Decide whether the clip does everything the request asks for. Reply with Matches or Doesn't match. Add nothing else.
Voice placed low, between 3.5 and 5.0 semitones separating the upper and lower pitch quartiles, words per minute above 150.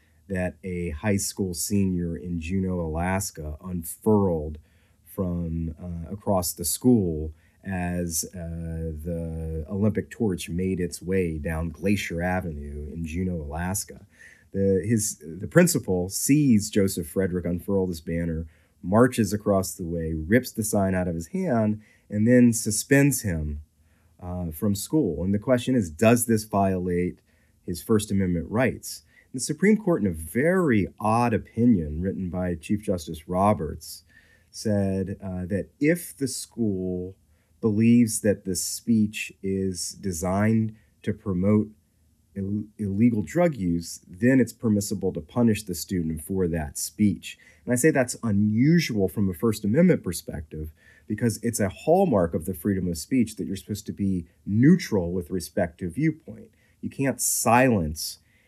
Doesn't match